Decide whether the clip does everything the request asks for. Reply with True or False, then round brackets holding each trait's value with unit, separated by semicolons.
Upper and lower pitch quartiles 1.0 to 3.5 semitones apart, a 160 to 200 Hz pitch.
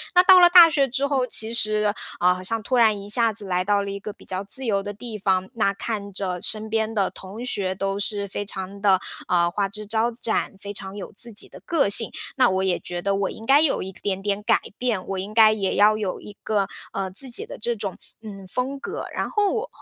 False (3.1 semitones; 210 Hz)